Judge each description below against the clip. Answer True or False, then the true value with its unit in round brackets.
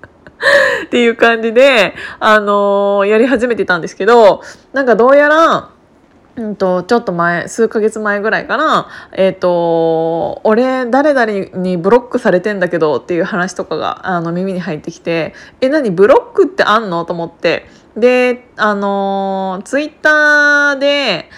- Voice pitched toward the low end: False (215 Hz)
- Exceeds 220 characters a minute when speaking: True (290 characters per minute)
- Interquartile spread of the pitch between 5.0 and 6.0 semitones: True (5.3 semitones)